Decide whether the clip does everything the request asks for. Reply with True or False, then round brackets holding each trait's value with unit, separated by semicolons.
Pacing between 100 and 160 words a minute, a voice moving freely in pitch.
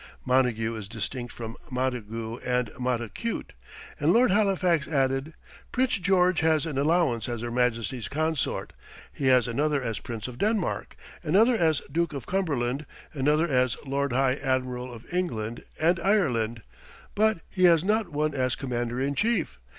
True (150 wpm; 5.8 semitones)